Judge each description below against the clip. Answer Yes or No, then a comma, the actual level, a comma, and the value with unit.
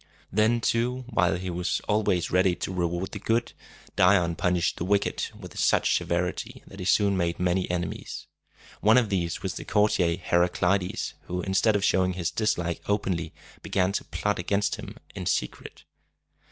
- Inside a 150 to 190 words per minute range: Yes, average, 170 wpm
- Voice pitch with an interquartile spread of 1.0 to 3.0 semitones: Yes, narrow, 2.6 semitones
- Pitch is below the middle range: Yes, very low, 95 Hz